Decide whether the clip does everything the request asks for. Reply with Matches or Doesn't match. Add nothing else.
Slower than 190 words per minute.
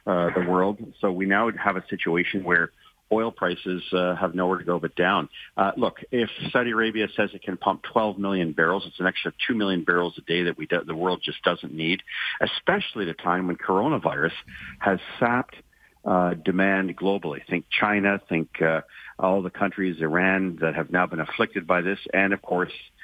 Doesn't match